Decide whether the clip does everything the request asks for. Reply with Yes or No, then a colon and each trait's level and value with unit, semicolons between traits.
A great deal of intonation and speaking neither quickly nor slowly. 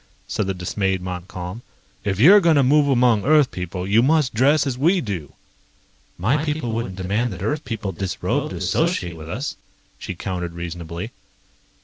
Yes: wide, 7.3 semitones; average, 165 wpm